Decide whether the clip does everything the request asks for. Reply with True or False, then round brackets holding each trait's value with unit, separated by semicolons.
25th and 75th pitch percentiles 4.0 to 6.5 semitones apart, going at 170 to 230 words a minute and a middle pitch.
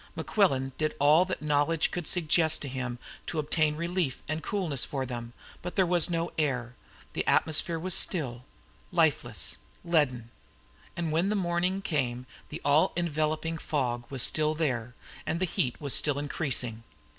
False (4.3 semitones; 155 wpm; 155 Hz)